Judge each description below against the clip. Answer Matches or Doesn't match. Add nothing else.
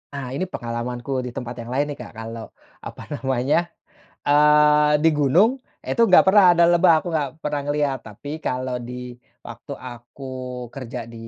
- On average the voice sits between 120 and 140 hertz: Matches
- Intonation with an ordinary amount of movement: Matches